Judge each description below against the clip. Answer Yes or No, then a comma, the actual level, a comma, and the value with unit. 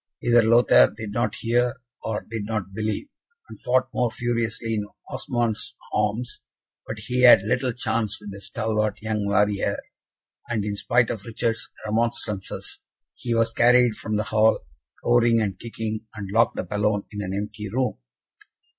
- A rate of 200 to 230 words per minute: No, average, 155 wpm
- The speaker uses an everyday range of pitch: No, narrow, 2.1 semitones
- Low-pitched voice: Yes, low, 110 Hz